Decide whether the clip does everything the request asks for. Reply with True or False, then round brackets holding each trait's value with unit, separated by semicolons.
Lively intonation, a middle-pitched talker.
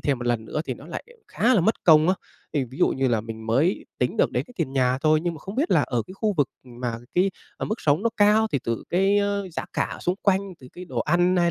True (7.2 semitones; 160 Hz)